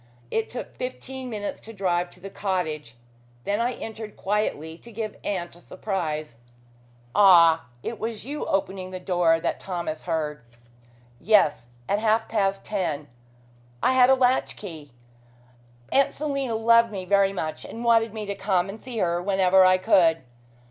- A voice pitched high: Yes, high, 195 Hz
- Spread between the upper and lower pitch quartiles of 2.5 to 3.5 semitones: No, average, 4.4 semitones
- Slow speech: No, average, 160 wpm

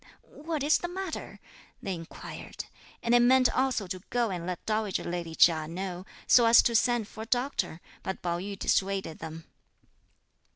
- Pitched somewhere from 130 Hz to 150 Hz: No, high, 200 Hz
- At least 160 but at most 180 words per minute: Yes, average, 170 wpm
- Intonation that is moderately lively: No, wide, 5.7 semitones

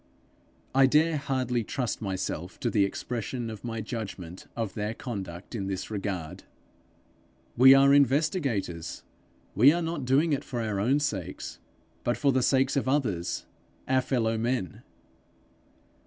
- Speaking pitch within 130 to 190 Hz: No, low, 120 Hz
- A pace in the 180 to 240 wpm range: No, average, 140 wpm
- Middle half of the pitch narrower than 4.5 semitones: No, average, 5.0 semitones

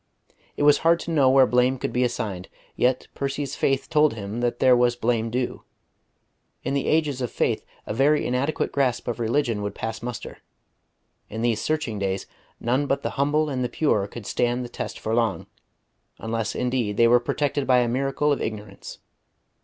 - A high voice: No, low, 125 Hz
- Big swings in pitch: No, average, 3.2 semitones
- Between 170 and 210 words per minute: Yes, average, 185 wpm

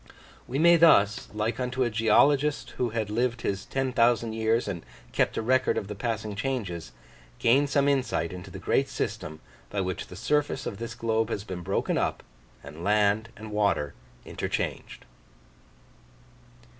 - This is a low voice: Yes, low, 110 Hz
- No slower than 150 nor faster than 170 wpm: Yes, average, 160 wpm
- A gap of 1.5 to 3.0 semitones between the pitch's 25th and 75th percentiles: No, average, 4.0 semitones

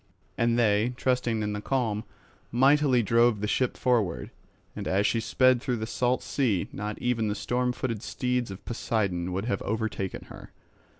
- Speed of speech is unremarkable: Yes, average, 170 wpm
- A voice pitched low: Yes, low, 115 Hz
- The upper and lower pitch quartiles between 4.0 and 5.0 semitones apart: No, average, 3.1 semitones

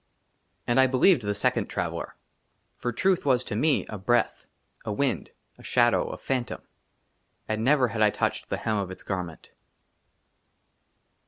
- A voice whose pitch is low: Yes, low, 120 Hz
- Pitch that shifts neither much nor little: Yes, average, 4.1 semitones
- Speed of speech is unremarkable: Yes, average, 155 wpm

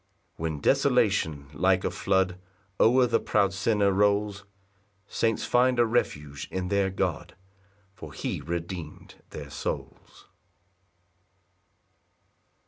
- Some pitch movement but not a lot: Yes, average, 4.1 semitones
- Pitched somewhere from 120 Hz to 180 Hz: No, very low, 95 Hz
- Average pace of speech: No, slow, 110 wpm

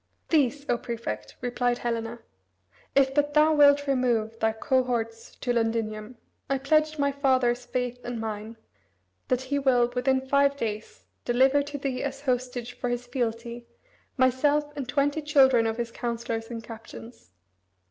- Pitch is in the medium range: No, very high, 250 Hz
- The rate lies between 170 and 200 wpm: No, average, 145 wpm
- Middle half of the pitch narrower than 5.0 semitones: Yes, average, 3.1 semitones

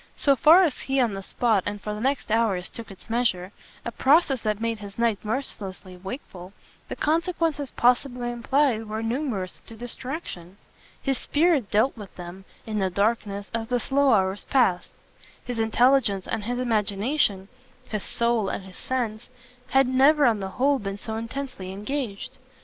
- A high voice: Yes, high, 230 Hz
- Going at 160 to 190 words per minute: Yes, average, 165 wpm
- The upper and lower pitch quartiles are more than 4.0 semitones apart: Yes, average, 4.8 semitones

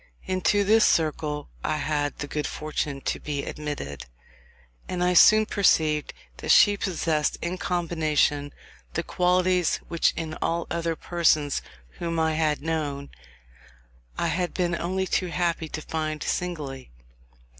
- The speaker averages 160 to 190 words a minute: No, slow, 135 wpm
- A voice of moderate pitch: Yes, medium, 160 Hz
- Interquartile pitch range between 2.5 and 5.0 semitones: Yes, average, 2.9 semitones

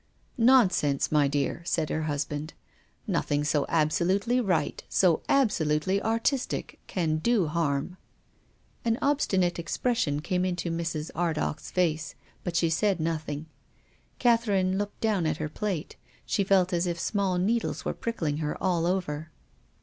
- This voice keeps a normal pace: Yes, average, 145 wpm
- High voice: No, medium, 175 Hz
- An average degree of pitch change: Yes, average, 4.4 semitones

